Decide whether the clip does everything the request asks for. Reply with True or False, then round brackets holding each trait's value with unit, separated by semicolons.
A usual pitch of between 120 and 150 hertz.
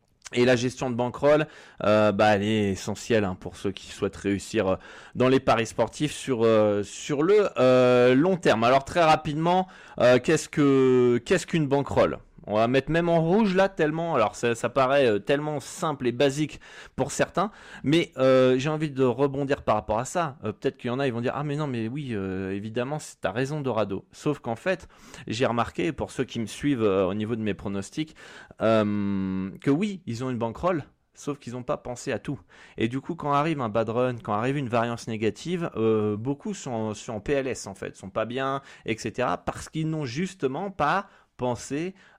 True (130 Hz)